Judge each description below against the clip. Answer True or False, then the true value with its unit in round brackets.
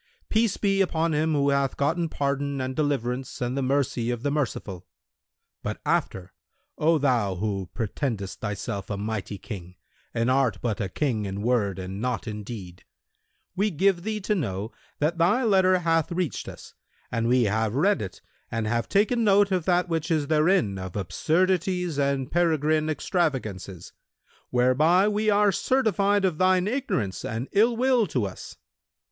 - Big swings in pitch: True (8.5 semitones)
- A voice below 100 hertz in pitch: False (140 Hz)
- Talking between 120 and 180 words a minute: True (165 wpm)